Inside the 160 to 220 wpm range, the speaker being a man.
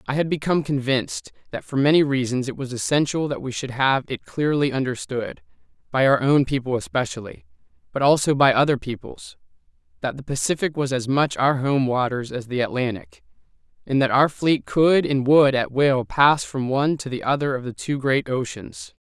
Yes: average, 190 wpm; male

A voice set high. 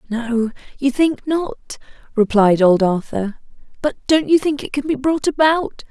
Yes: very high, 260 Hz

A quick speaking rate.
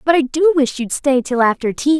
Yes: fast, 270 wpm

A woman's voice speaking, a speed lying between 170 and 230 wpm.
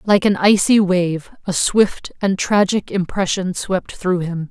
No: female; average, 160 wpm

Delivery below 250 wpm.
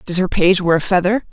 No: fast, 275 wpm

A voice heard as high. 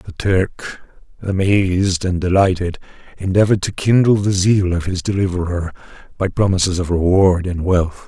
No: very low, 95 Hz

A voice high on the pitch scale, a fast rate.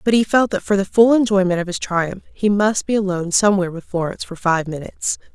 Yes: high, 195 Hz; fast, 235 wpm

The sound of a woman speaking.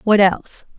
Yes: female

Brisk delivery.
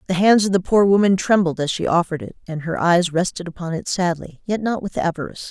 Yes: fast, 240 wpm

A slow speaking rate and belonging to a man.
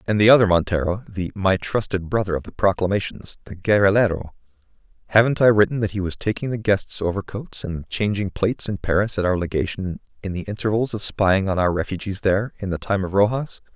No: average, 190 wpm; male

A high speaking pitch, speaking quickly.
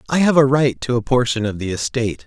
No: low, 120 Hz; fast, 265 wpm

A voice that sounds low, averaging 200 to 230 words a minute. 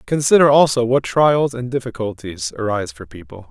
No: low, 130 Hz; average, 155 wpm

